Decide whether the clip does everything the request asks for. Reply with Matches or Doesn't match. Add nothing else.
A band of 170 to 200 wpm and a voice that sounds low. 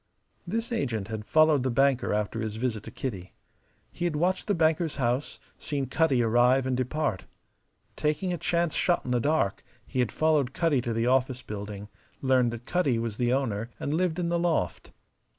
Matches